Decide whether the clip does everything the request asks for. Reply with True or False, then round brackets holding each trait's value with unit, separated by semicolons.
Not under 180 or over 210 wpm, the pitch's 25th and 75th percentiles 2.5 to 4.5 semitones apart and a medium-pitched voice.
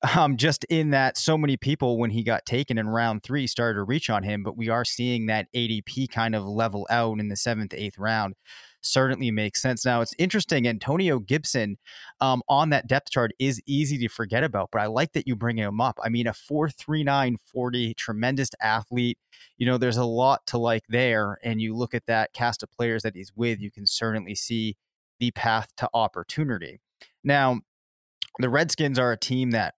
False (205 wpm; 3.1 semitones; 120 Hz)